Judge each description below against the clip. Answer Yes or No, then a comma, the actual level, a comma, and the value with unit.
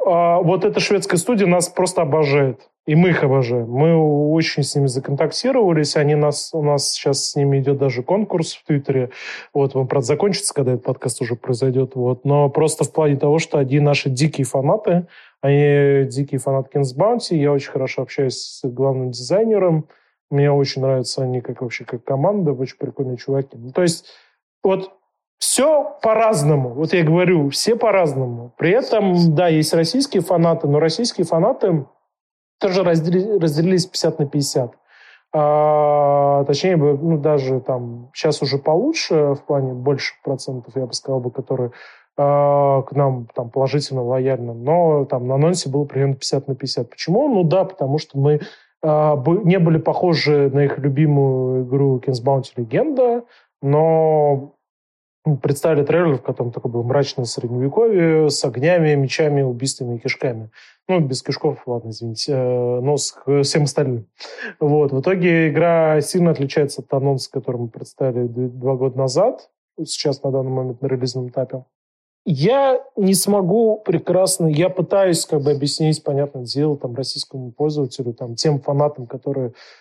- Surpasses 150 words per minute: Yes, fast, 160 wpm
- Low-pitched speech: No, medium, 145 Hz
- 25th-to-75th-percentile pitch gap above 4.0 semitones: No, average, 3.6 semitones